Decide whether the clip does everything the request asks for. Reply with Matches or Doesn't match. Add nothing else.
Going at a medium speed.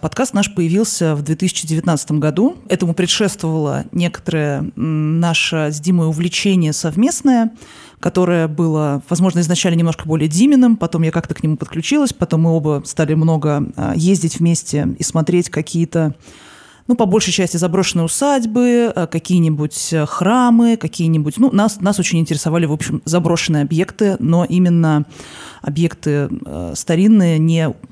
Matches